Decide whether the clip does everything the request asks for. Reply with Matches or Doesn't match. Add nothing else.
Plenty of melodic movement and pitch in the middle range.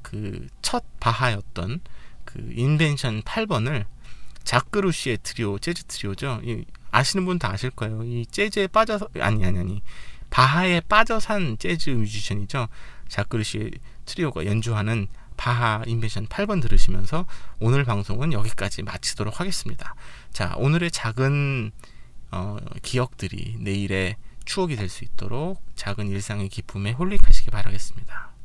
Doesn't match